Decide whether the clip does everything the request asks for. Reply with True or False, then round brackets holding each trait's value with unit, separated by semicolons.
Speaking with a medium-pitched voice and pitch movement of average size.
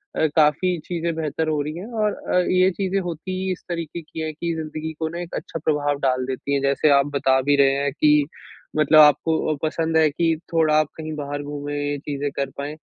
False (155 Hz; 2.3 semitones)